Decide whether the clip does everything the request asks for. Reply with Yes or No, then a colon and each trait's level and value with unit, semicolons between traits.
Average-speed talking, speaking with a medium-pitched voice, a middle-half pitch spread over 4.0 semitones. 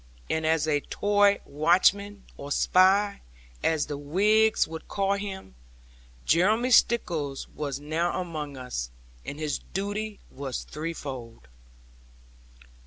No: slow, 110 wpm; medium, 165 Hz; wide, 5.6 semitones